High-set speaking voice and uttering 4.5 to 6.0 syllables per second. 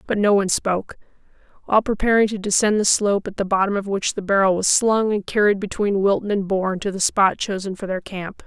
Yes: high, 200 Hz; 5.9 syllables/s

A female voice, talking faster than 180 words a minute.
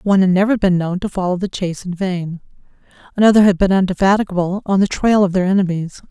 Yes: female; fast, 205 wpm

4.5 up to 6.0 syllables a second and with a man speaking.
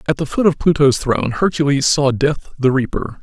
Yes: 5.3 syllables/s; male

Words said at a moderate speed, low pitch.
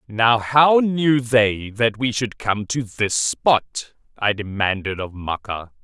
Yes: average, 155 wpm; low, 115 Hz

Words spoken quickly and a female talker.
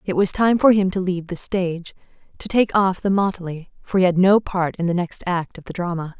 Yes: fast, 250 wpm; female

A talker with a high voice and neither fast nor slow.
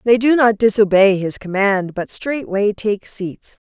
Yes: high, 205 Hz; average, 165 wpm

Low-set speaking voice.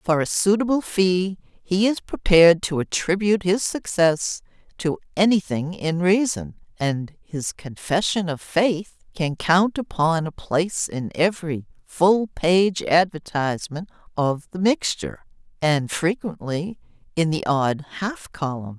No: medium, 175 Hz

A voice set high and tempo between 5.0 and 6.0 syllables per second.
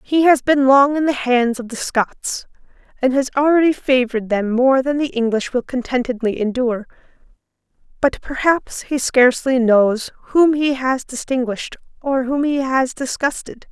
No: very high, 260 Hz; 4.7 syllables/s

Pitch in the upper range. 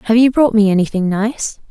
Yes: high, 220 Hz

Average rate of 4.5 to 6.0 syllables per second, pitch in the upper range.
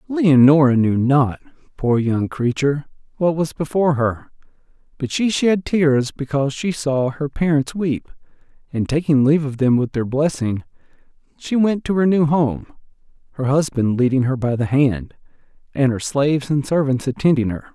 No: 4.8 syllables/s; medium, 140 Hz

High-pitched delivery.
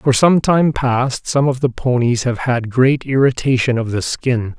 No: low, 130 Hz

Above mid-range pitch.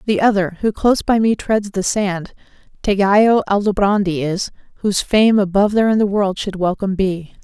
Yes: high, 200 Hz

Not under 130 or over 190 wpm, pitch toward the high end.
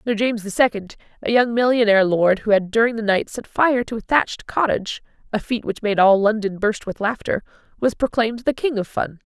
No: fast, 205 wpm; high, 220 Hz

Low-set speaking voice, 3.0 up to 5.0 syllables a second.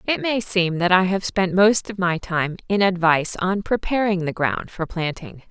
No: medium, 185 Hz; 4.6 syllables/s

